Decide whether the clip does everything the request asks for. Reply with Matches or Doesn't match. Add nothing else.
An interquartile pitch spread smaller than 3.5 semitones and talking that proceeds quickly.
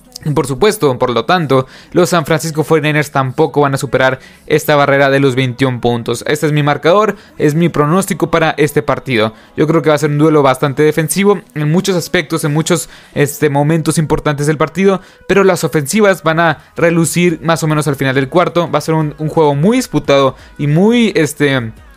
Matches